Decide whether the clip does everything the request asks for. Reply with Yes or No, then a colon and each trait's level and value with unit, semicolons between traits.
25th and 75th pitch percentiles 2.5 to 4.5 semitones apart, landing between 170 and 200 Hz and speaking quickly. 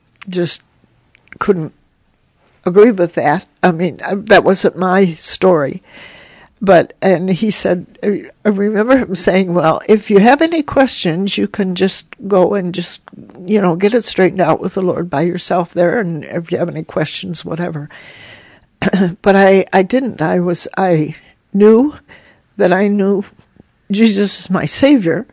No: average, 2.9 semitones; medium, 185 Hz; average, 155 wpm